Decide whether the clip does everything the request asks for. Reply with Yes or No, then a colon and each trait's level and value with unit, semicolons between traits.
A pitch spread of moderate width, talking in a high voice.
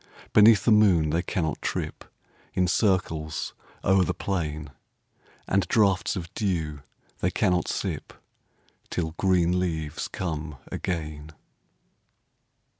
No: average, 3.5 semitones; very low, 90 Hz